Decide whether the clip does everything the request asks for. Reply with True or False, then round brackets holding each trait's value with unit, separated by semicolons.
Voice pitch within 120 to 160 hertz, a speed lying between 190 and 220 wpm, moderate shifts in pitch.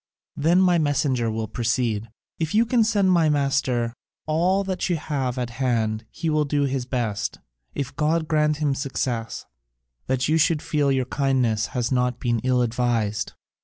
False (135 Hz; 165 wpm; 4.4 semitones)